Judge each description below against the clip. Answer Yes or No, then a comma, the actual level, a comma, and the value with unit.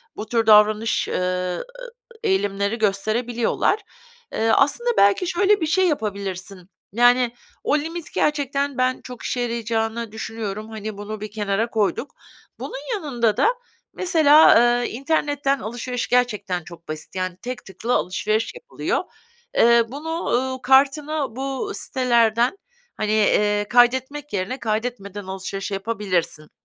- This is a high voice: Yes, high, 235 Hz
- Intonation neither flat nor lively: Yes, average, 4.9 semitones